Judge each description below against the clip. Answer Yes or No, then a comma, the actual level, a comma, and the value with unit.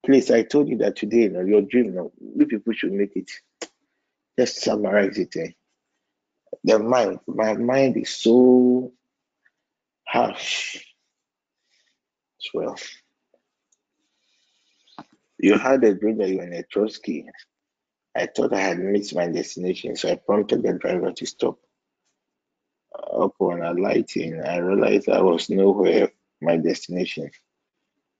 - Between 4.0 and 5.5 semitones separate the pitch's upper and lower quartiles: Yes, average, 4.5 semitones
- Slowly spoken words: Yes, slow, 130 wpm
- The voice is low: Yes, low, 110 Hz